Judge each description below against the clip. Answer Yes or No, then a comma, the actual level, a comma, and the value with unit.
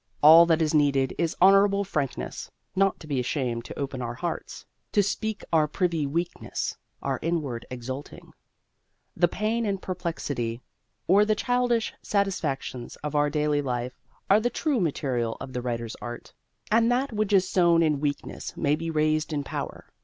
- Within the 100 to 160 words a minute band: No, average, 170 wpm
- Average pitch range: No, wide, 6.2 semitones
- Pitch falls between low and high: Yes, medium, 155 Hz